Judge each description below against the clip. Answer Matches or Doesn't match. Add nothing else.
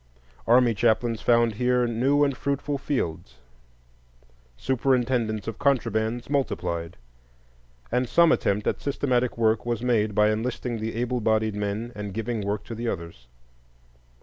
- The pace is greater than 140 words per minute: Doesn't match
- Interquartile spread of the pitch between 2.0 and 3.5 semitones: Matches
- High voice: Doesn't match